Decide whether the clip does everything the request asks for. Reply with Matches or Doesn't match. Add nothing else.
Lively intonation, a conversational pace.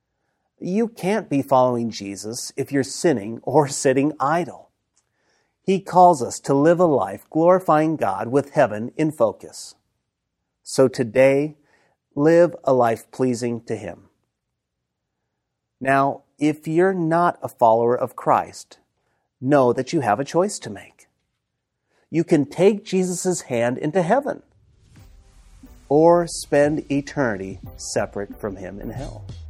Doesn't match